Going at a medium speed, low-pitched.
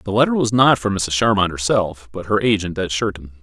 No: fast, 230 wpm; low, 100 Hz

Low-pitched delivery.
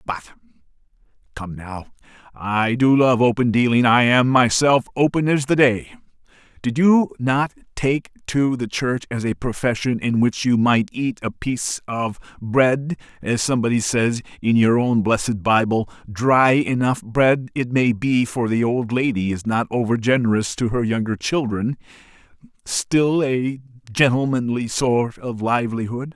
Yes: low, 120 Hz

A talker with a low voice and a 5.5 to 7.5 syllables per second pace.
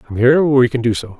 Yes: low, 125 Hz; 6.1 syllables/s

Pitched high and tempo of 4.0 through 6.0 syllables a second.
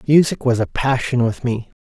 No: low, 125 Hz; 5.0 syllables/s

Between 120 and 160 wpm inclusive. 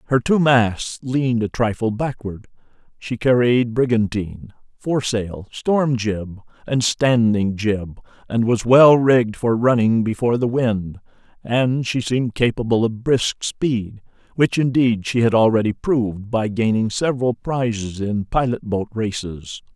Yes: average, 140 wpm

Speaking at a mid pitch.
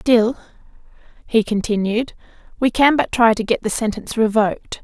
No: high, 225 Hz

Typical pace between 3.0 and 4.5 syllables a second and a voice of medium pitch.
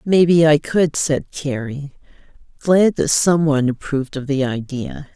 Yes: 4.4 syllables/s; medium, 145 Hz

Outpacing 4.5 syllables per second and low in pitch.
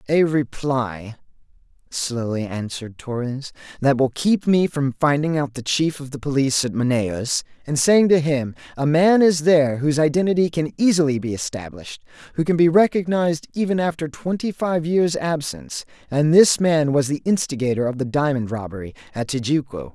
No: 5.2 syllables/s; medium, 145 Hz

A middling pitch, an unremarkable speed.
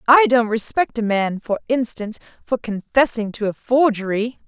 No: high, 230 Hz; average, 160 wpm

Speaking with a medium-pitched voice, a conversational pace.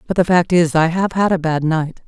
No: medium, 170 Hz; fast, 290 wpm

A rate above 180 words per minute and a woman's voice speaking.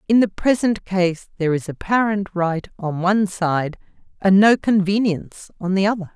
No: average, 165 wpm; female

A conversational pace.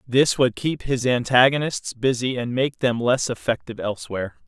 Yes: average, 160 wpm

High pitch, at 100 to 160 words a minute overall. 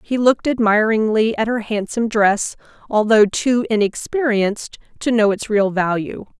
Yes: high, 220 Hz; average, 140 wpm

